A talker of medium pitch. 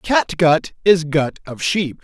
Yes: medium, 165 Hz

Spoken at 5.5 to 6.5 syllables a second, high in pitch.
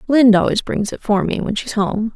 Yes: 5.6 syllables/s; high, 220 Hz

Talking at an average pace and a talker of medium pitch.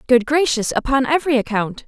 No: average, 160 wpm; very high, 260 Hz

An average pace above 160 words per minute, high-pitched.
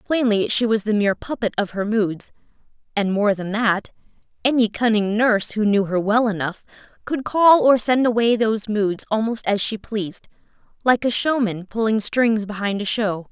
Yes: average, 180 wpm; high, 215 Hz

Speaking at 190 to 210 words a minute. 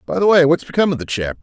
No: fast, 335 wpm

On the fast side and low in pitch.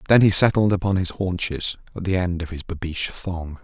Yes: fast, 215 wpm; very low, 90 Hz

